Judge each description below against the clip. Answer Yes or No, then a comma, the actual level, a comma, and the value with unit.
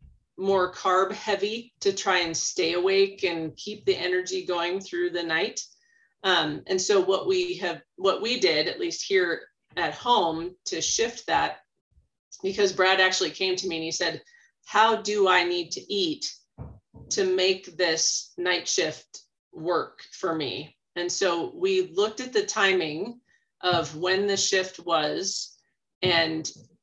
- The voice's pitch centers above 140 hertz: Yes, high, 190 Hz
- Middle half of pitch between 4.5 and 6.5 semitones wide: Yes, wide, 5.4 semitones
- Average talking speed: Yes, average, 155 wpm